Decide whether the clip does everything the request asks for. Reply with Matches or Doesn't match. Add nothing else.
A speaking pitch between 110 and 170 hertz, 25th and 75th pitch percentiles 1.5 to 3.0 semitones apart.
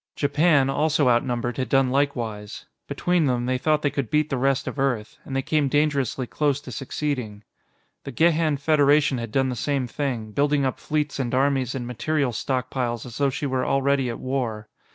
Matches